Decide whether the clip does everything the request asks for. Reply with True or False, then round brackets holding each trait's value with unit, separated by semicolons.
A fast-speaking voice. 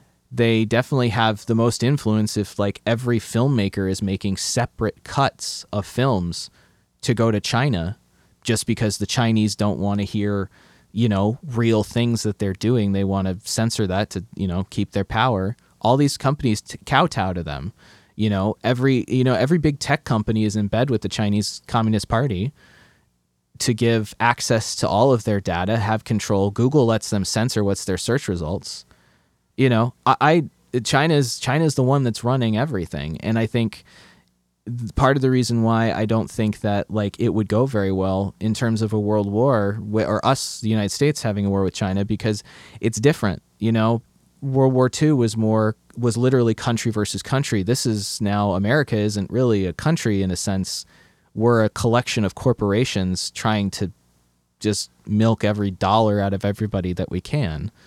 False (185 wpm)